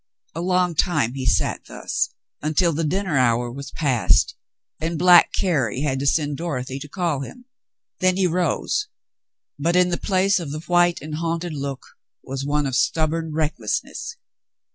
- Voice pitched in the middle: Yes, medium, 155 Hz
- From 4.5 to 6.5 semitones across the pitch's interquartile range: No, average, 4.0 semitones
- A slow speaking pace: No, average, 165 wpm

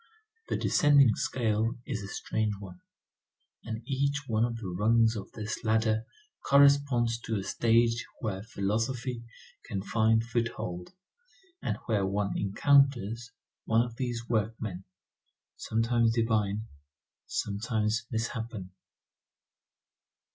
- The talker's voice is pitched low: Yes, low, 115 Hz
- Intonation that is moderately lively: No, narrow, 2.0 semitones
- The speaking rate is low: Yes, slow, 110 wpm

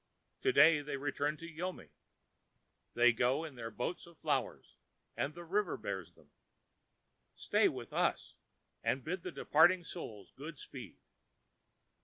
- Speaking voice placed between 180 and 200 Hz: No, medium, 150 Hz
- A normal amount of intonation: No, wide, 5.8 semitones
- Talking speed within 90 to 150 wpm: Yes, slow, 135 wpm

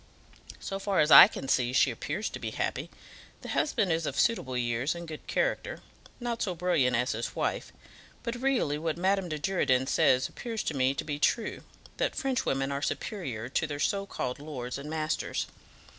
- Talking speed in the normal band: Yes, average, 190 wpm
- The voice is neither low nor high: Yes, medium, 155 Hz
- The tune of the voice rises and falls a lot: Yes, wide, 6.9 semitones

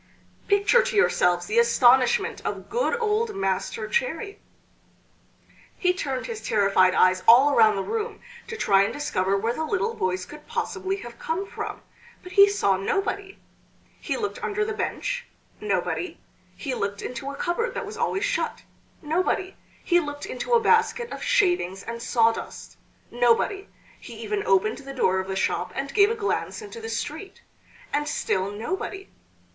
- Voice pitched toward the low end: No, very high, 300 Hz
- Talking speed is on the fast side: No, average, 160 wpm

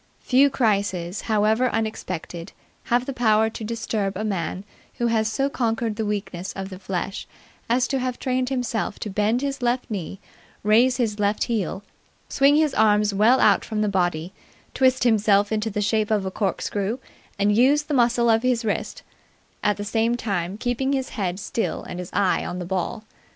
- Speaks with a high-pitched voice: Yes, high, 220 Hz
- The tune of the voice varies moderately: Yes, average, 3.4 semitones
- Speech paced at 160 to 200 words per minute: Yes, average, 180 wpm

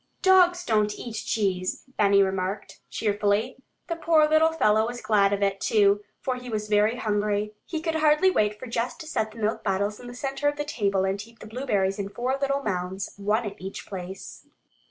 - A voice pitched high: Yes, high, 215 Hz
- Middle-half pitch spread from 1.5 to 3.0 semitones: No, average, 4.6 semitones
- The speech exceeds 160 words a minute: Yes, average, 200 wpm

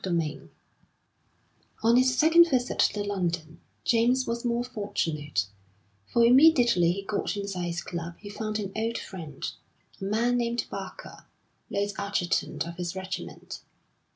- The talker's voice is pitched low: No, high, 205 Hz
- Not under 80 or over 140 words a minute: Yes, slow, 135 wpm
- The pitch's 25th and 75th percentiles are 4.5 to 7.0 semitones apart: Yes, average, 5.1 semitones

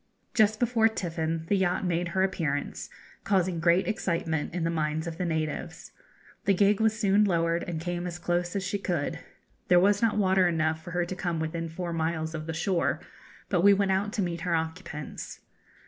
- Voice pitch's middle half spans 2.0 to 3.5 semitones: Yes, average, 2.8 semitones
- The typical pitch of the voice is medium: Yes, medium, 175 Hz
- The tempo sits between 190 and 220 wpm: Yes, average, 195 wpm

